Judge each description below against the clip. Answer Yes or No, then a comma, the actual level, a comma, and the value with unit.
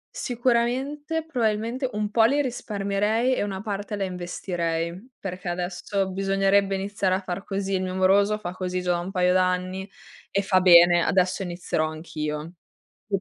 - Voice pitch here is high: Yes, high, 195 Hz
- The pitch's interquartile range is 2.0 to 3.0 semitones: Yes, average, 2.7 semitones